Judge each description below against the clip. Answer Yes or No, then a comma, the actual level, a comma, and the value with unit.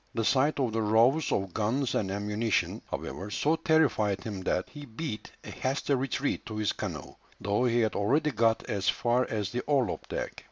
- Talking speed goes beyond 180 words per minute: Yes, average, 190 wpm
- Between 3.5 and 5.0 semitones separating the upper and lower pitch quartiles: Yes, average, 4.6 semitones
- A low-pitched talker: Yes, low, 115 Hz